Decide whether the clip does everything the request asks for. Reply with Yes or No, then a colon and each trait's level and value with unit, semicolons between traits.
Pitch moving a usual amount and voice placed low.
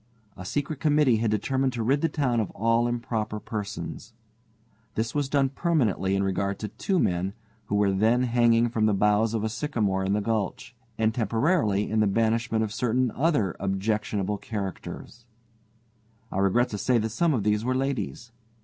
Yes: average, 3.3 semitones; low, 110 Hz